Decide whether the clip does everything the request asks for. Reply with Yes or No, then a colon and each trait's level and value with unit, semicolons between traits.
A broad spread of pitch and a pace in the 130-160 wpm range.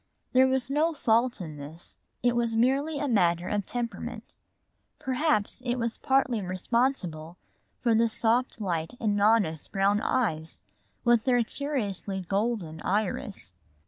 No: average, 5.0 semitones; slow, 135 wpm